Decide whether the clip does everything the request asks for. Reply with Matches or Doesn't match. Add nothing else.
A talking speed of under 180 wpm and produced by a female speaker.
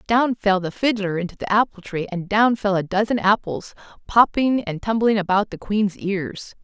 Doesn't match